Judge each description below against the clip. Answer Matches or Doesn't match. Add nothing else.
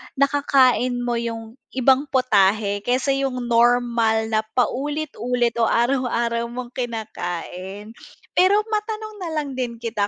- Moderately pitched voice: Doesn't match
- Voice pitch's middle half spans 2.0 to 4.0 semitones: Matches